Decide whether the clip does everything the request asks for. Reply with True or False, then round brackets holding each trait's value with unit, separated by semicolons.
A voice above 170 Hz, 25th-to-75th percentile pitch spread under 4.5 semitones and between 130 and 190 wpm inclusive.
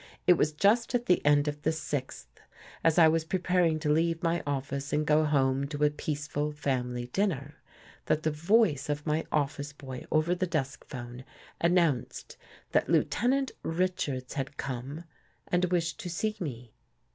False (150 Hz; 3.4 semitones; 165 wpm)